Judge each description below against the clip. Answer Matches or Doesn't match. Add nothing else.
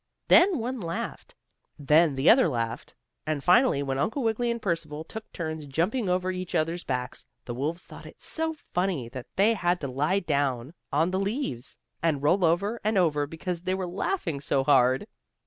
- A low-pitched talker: Doesn't match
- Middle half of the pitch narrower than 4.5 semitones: Doesn't match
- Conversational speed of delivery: Matches